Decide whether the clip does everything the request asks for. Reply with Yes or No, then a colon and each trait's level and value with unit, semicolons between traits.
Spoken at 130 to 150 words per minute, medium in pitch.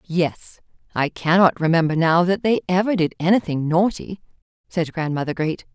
Yes: average, 145 wpm; medium, 170 Hz